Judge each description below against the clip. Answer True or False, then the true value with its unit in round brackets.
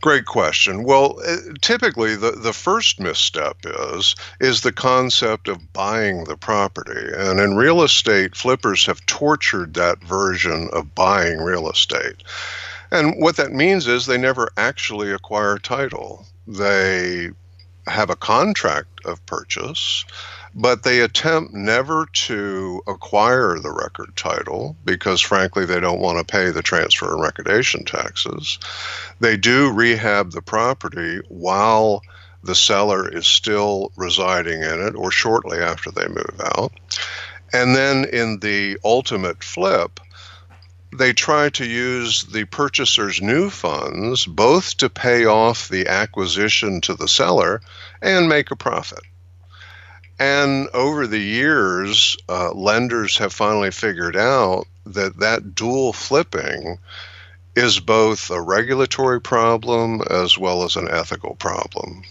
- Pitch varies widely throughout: False (5.0 semitones)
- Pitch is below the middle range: True (105 Hz)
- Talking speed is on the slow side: True (130 wpm)